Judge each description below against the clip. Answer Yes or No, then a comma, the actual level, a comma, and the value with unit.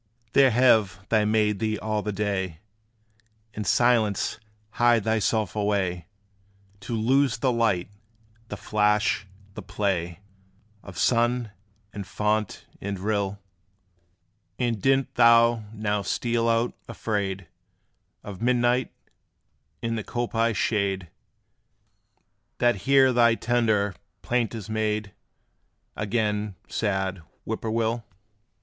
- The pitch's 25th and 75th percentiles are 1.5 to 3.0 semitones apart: Yes, narrow, 2.6 semitones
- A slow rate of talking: Yes, slow, 110 wpm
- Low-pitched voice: Yes, low, 110 Hz